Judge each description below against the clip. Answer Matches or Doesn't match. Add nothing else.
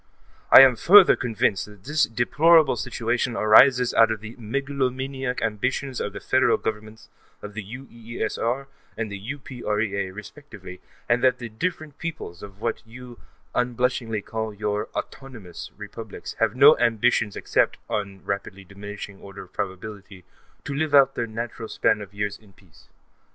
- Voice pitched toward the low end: Matches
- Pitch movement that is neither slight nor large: Matches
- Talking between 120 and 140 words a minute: Doesn't match